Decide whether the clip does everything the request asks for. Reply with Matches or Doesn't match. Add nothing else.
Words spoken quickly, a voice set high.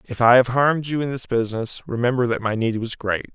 Doesn't match